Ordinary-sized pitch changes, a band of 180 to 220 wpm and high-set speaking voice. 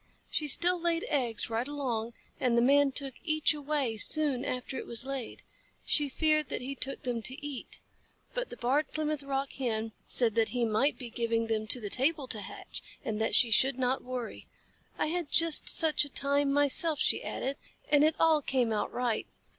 Yes: average, 4.0 semitones; average, 195 wpm; very high, 270 Hz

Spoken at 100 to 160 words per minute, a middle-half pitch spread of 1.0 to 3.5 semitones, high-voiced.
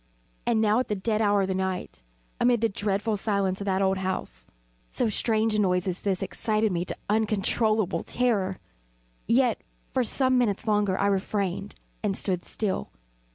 No: average, 170 wpm; narrow, 2.5 semitones; high, 205 Hz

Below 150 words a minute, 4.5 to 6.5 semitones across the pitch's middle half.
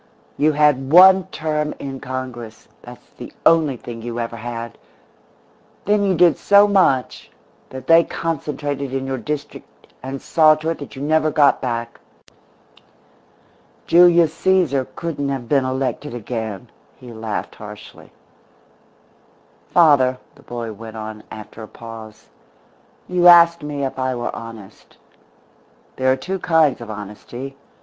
Yes: average, 140 wpm; average, 5.1 semitones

